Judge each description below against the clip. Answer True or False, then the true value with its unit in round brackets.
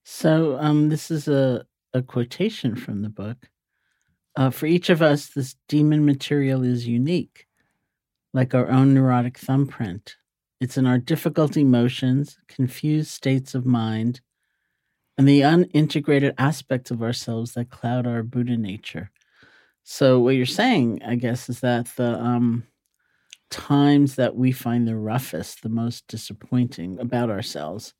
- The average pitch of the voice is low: True (125 Hz)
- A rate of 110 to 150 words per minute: True (140 wpm)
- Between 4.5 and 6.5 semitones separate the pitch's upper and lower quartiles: False (2.9 semitones)